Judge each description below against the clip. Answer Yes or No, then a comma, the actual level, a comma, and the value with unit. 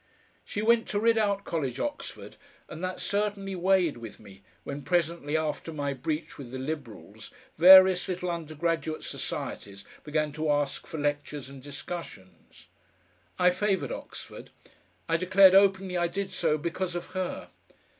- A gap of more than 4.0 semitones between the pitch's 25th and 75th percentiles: Yes, average, 4.4 semitones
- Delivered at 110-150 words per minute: Yes, average, 145 wpm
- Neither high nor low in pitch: Yes, medium, 165 Hz